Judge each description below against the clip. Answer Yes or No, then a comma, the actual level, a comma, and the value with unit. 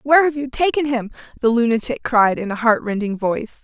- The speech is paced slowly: No, average, 200 wpm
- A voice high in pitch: Yes, high, 245 Hz